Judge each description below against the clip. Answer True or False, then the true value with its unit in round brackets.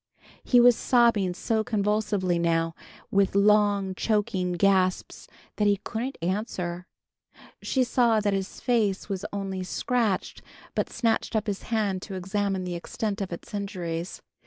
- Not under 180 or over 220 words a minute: False (140 wpm)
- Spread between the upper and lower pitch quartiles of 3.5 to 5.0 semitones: False (2.8 semitones)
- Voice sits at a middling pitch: False (200 Hz)